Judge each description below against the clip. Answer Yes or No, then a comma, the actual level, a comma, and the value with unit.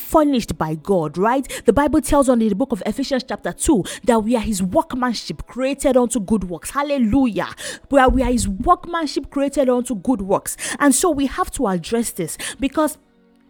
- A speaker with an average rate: Yes, average, 190 wpm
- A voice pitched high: Yes, very high, 255 Hz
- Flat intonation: No, average, 3.8 semitones